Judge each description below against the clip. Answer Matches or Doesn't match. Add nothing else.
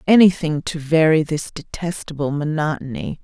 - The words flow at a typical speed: Doesn't match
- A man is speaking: Doesn't match